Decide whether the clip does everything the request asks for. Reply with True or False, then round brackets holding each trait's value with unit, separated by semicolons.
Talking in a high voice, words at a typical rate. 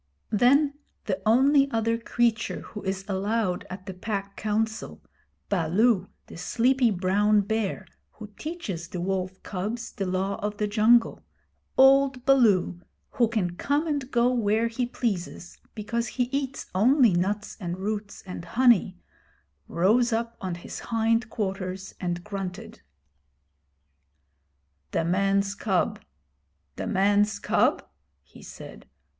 False (210 Hz; 125 wpm)